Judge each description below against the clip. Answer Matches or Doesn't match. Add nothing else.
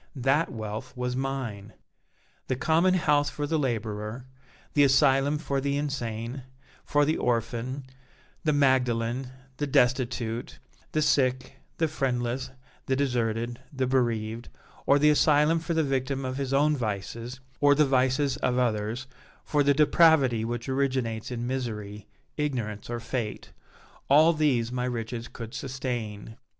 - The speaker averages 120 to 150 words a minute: Matches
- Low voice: Matches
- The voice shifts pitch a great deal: Doesn't match